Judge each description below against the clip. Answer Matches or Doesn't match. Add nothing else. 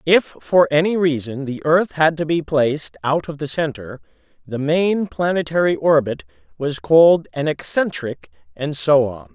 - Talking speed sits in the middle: Matches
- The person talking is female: Doesn't match